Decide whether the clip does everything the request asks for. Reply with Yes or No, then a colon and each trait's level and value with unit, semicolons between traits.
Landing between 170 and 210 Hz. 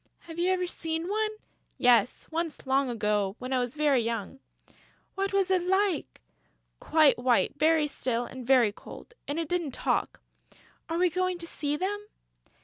No: very high, 310 Hz